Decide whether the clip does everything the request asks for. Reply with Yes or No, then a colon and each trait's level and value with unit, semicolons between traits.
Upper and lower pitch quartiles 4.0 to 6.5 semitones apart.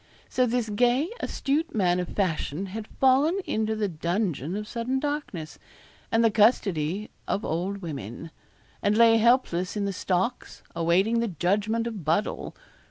Yes: average, 4.8 semitones